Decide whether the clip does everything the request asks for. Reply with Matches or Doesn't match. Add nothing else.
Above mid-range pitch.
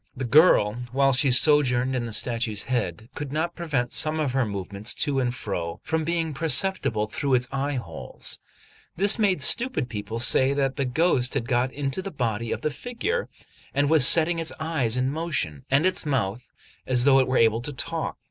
Doesn't match